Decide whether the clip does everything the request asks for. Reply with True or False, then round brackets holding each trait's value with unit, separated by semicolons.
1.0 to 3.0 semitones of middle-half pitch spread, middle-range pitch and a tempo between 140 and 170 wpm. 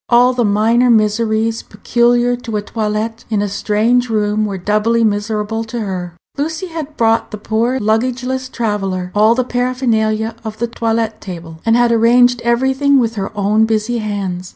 False (2.4 semitones; 225 Hz; 165 wpm)